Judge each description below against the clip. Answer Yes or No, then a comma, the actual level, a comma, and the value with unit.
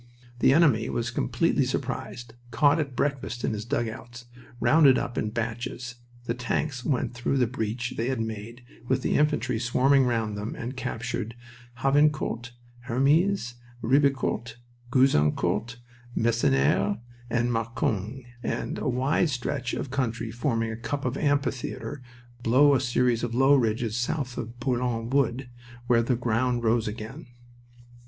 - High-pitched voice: No, low, 120 Hz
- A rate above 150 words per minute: No, average, 140 wpm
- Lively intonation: No, narrow, 2.5 semitones